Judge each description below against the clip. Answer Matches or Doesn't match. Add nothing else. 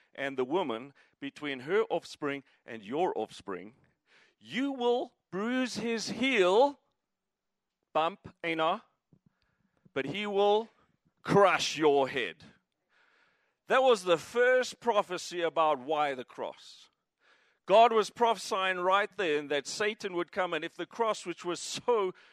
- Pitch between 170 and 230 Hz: Matches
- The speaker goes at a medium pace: Doesn't match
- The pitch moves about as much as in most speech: Doesn't match